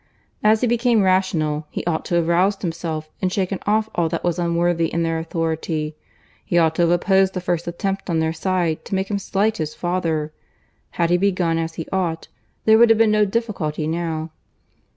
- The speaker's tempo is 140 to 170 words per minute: No, average, 200 wpm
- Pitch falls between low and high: Yes, medium, 175 Hz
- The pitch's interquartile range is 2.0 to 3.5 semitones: Yes, average, 3.0 semitones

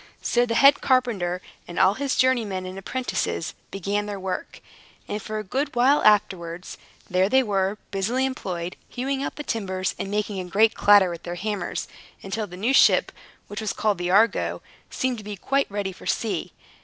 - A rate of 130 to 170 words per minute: No, average, 185 wpm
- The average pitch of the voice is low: No, high, 205 Hz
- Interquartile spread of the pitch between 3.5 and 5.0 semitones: Yes, average, 4.3 semitones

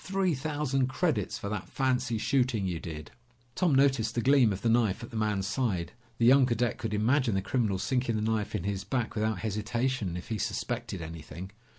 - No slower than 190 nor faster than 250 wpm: Yes, average, 200 wpm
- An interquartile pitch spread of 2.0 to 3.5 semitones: No, average, 4.3 semitones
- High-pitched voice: No, low, 115 Hz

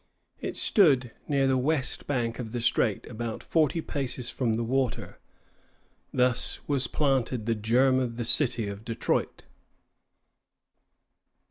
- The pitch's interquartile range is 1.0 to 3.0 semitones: Yes, narrow, 2.5 semitones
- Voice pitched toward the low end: Yes, low, 125 Hz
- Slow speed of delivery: Yes, slow, 130 wpm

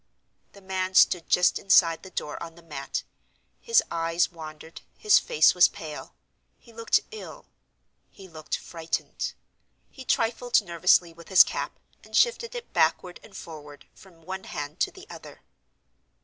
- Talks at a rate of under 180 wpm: Yes, average, 150 wpm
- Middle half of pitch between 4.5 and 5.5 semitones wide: Yes, average, 5.2 semitones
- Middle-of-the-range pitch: Yes, medium, 180 Hz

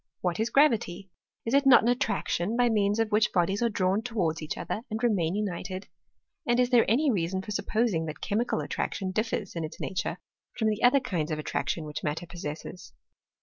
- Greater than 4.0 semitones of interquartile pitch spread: Yes, average, 4.9 semitones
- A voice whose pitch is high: Yes, high, 205 Hz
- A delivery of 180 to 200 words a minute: Yes, average, 195 wpm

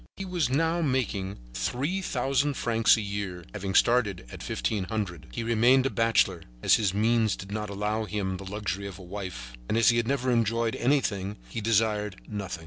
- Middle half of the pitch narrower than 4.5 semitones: Yes, average, 3.5 semitones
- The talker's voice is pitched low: Yes, low, 110 Hz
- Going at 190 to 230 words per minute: Yes, average, 195 wpm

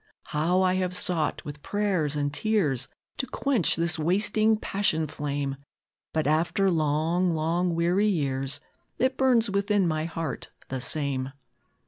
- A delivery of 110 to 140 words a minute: Yes, slow, 135 wpm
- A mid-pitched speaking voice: Yes, medium, 165 Hz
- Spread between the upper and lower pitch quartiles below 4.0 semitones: No, average, 4.9 semitones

